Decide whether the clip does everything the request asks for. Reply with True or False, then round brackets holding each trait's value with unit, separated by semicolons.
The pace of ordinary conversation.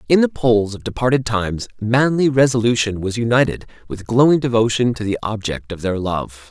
True (175 wpm)